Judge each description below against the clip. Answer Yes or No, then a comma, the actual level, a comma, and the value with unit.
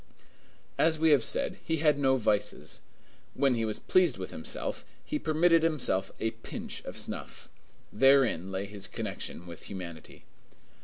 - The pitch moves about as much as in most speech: No, wide, 7.7 semitones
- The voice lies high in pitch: No, low, 130 Hz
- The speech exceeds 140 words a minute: Yes, average, 150 wpm